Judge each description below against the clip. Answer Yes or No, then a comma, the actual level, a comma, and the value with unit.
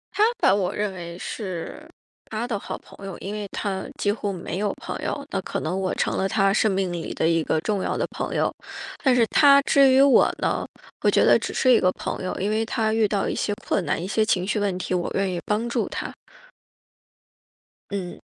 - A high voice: Yes, high, 200 Hz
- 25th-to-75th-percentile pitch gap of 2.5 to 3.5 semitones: Yes, average, 3.0 semitones